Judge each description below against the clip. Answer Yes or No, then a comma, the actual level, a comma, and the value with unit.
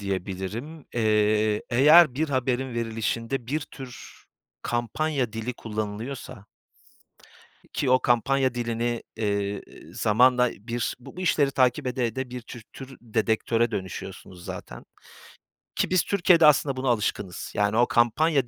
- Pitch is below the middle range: Yes, low, 120 Hz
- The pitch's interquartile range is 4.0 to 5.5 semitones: No, average, 3.4 semitones